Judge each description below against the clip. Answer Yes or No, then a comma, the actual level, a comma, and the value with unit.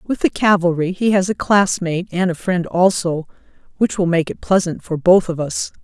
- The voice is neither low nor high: Yes, medium, 180 Hz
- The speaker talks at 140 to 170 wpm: No, fast, 205 wpm